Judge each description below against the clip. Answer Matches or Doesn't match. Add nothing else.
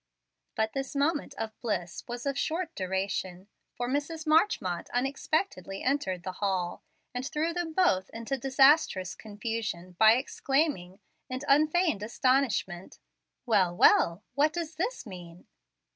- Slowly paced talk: Matches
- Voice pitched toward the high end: Matches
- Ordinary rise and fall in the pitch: Doesn't match